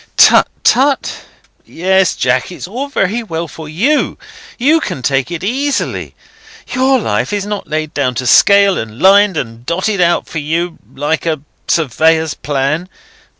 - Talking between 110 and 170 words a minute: Yes, average, 150 wpm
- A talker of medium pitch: Yes, medium, 170 Hz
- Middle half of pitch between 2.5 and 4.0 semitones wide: No, wide, 5.5 semitones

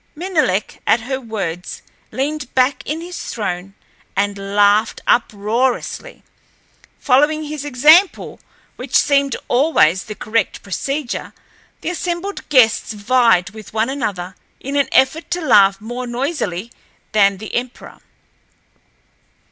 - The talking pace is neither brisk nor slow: No, slow, 115 wpm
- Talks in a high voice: Yes, high, 245 Hz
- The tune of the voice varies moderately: No, wide, 5.9 semitones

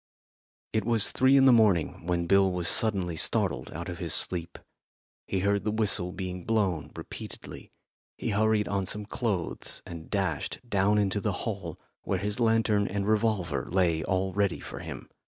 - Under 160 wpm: No, average, 170 wpm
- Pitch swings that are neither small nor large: Yes, average, 3.2 semitones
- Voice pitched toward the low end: Yes, low, 100 Hz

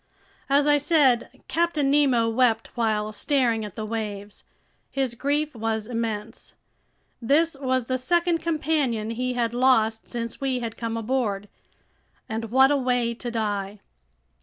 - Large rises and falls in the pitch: No, average, 3.6 semitones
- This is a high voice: Yes, high, 240 Hz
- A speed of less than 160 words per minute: Yes, average, 140 wpm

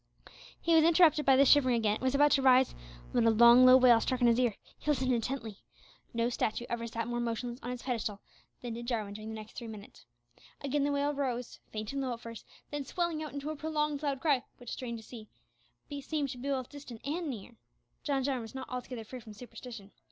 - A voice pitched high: Yes, very high, 250 Hz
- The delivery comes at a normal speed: No, fast, 230 wpm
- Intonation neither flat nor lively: Yes, average, 3.4 semitones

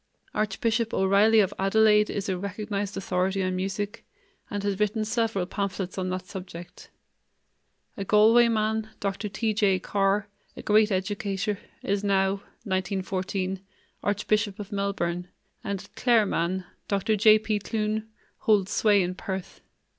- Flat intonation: Yes, narrow, 1.9 semitones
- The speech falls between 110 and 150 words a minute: Yes, average, 140 wpm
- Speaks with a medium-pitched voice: No, high, 200 Hz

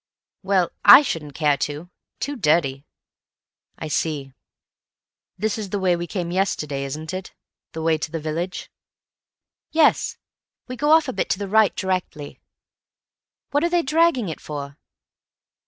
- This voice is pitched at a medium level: Yes, medium, 175 Hz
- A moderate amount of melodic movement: No, wide, 6.2 semitones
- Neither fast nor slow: Yes, average, 150 wpm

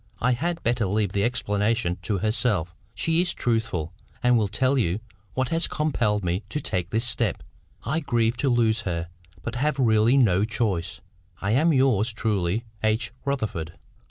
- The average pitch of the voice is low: Yes, low, 115 Hz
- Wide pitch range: No, average, 4.1 semitones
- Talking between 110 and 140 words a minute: No, average, 165 wpm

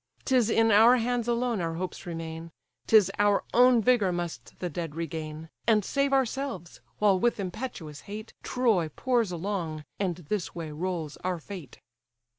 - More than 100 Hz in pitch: Yes, high, 190 Hz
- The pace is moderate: Yes, average, 155 wpm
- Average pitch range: No, wide, 5.9 semitones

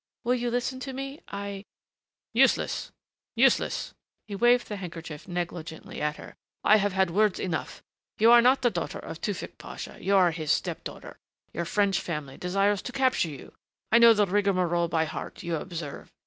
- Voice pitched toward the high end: Yes, high, 195 Hz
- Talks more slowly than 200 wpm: Yes, average, 180 wpm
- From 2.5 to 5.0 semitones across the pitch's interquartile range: No, wide, 5.4 semitones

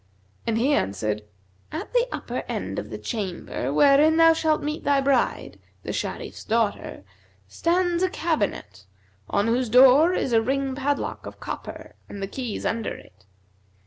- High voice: Yes, very high, 265 Hz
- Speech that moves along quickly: No, average, 155 wpm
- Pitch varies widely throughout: Yes, wide, 6.9 semitones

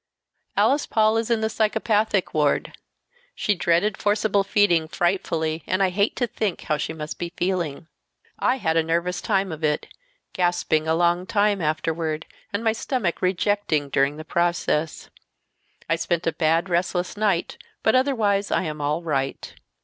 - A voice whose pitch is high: No, medium, 175 Hz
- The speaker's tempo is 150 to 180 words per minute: Yes, average, 160 wpm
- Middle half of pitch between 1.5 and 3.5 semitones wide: No, average, 4.3 semitones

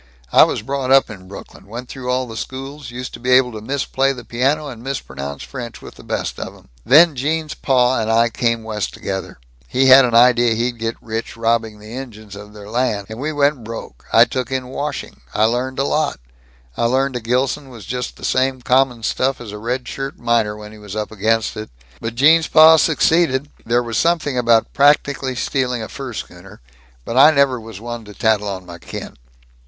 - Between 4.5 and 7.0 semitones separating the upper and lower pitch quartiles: No, average, 3.2 semitones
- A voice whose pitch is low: Yes, low, 125 Hz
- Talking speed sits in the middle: No, fast, 210 wpm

